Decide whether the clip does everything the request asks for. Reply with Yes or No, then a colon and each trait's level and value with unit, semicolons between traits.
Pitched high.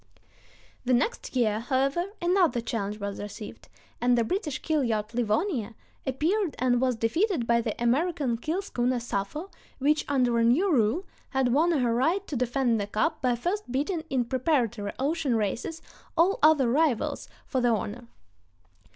Yes: very high, 255 Hz